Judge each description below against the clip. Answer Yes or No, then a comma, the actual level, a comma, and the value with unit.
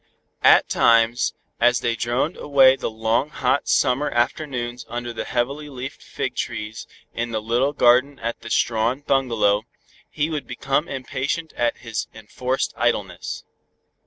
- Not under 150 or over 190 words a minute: No, average, 140 wpm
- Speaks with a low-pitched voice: Yes, low, 120 Hz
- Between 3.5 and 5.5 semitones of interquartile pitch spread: No, average, 2.9 semitones